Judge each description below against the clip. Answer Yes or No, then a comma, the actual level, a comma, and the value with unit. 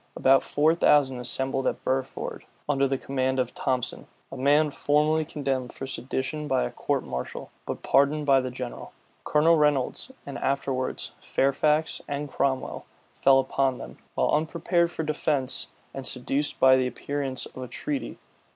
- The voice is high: No, low, 135 Hz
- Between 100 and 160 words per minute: Yes, average, 155 wpm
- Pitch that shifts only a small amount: Yes, narrow, 2.3 semitones